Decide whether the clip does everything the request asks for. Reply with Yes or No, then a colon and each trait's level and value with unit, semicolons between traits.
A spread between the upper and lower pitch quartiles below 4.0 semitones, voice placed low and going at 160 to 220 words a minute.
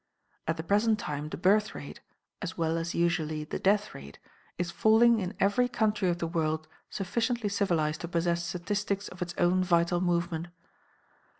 No: average, 3.4 semitones; medium, 175 Hz; average, 170 wpm